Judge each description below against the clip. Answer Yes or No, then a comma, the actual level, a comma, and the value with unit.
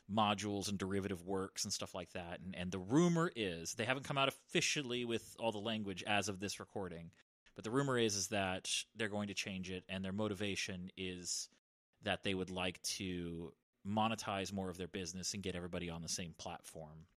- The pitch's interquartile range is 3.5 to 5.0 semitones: No, average, 2.7 semitones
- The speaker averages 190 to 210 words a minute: Yes, fast, 205 wpm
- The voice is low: Yes, very low, 95 Hz